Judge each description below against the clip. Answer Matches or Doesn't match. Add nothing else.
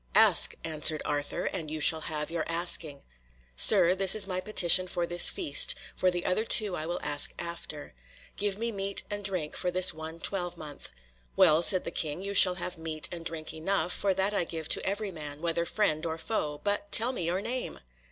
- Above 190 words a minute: Matches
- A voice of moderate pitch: Matches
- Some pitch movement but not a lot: Matches